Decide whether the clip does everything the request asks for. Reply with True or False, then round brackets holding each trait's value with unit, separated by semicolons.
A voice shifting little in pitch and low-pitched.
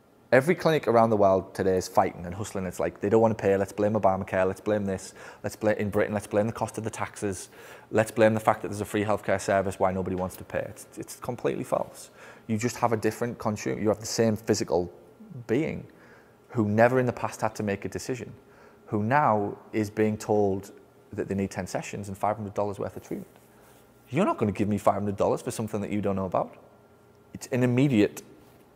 True (2.2 semitones; 105 Hz)